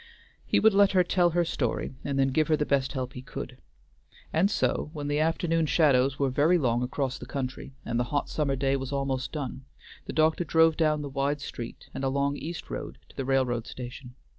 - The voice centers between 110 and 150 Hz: Yes, medium, 140 Hz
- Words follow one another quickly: Yes, fast, 215 wpm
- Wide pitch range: No, average, 3.1 semitones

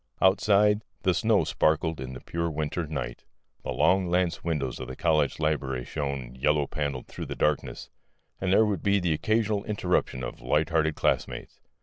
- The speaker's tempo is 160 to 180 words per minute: Yes, average, 175 wpm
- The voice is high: No, very low, 80 Hz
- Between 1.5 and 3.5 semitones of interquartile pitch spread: No, average, 4.9 semitones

